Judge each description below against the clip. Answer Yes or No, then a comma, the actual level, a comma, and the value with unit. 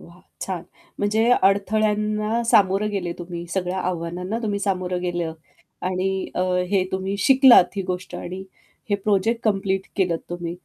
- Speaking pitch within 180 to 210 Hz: Yes, high, 190 Hz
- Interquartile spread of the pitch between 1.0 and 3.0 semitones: Yes, narrow, 2.6 semitones